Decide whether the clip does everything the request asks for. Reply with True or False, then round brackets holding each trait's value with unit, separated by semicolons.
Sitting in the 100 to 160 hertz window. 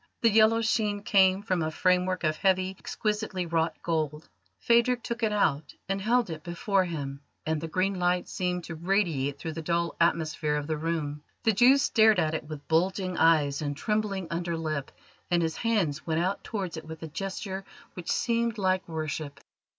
False (175 Hz)